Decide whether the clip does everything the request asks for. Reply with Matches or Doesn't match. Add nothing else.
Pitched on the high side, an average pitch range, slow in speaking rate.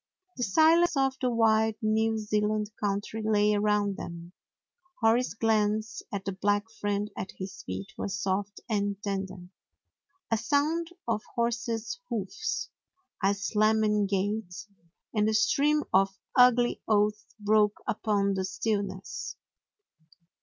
Doesn't match